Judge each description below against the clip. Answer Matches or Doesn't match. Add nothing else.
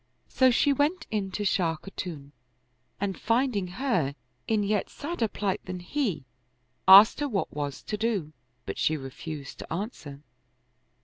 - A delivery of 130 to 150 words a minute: Matches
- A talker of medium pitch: Doesn't match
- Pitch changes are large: Matches